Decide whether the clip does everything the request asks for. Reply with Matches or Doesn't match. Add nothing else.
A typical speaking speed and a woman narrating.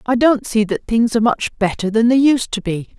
Doesn't match